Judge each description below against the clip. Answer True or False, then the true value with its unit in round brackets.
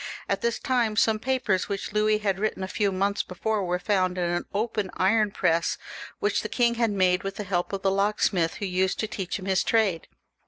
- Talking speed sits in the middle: False (220 wpm)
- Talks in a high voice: True (200 Hz)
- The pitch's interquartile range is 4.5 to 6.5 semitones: False (2.7 semitones)